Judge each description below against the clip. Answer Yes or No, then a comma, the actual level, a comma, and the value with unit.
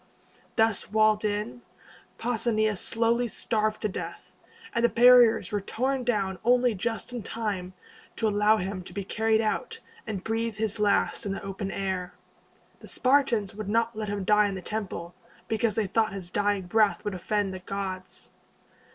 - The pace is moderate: Yes, average, 170 wpm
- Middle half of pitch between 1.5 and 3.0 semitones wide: Yes, narrow, 2.4 semitones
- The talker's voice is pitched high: Yes, high, 215 Hz